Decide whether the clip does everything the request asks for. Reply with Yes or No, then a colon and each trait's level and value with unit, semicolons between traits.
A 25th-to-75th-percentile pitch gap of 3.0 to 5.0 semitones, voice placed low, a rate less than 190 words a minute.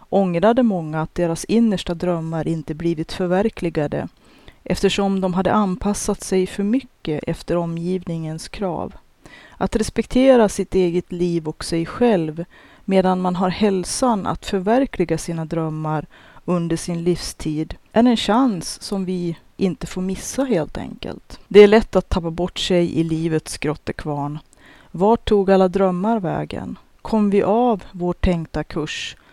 No: average, 3.5 semitones; medium, 185 Hz; average, 140 wpm